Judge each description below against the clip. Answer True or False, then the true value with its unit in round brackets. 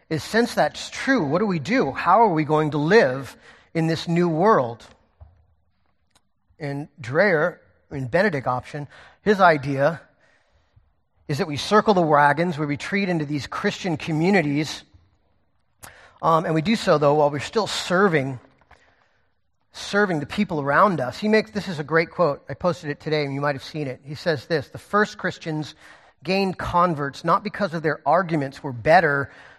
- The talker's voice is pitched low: False (155 Hz)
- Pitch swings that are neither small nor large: True (4.6 semitones)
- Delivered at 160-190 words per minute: True (170 wpm)